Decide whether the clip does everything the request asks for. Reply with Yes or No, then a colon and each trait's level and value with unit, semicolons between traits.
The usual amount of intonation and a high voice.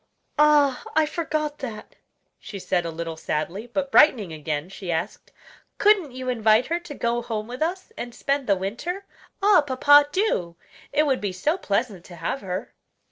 No: wide, 7.8 semitones; high, 245 Hz